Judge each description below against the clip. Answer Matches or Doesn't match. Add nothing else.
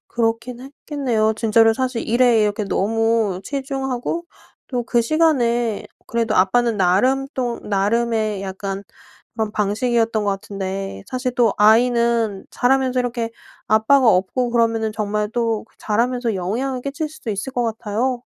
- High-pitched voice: Matches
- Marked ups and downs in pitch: Doesn't match